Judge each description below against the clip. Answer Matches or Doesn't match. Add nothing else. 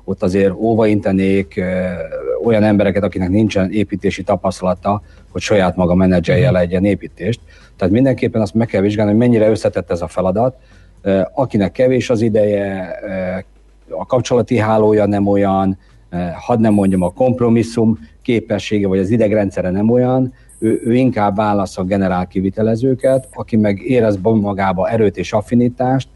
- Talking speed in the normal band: Matches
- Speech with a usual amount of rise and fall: Matches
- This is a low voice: Matches